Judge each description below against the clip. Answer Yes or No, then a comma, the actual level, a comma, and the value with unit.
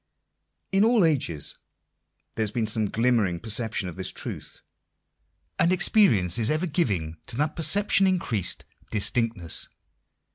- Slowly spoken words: Yes, slow, 130 wpm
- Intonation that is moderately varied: No, wide, 8.9 semitones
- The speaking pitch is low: Yes, low, 115 Hz